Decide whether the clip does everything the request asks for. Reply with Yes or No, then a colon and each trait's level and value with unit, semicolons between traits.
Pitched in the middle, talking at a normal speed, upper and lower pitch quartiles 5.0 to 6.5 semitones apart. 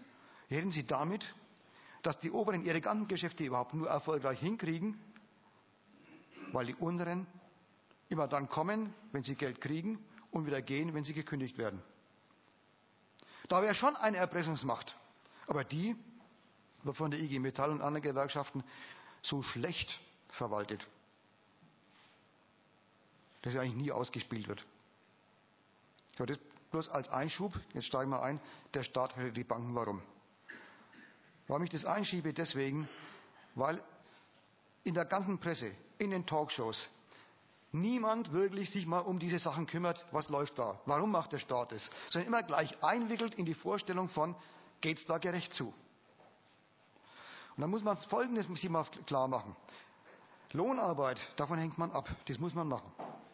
Yes: medium, 160 Hz; average, 140 wpm; average, 5.3 semitones